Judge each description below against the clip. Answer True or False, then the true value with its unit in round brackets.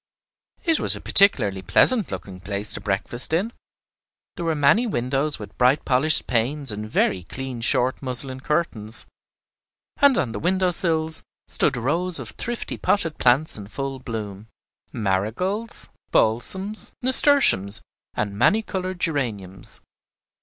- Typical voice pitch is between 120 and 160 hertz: True (135 Hz)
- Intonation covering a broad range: True (8.4 semitones)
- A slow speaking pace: True (130 wpm)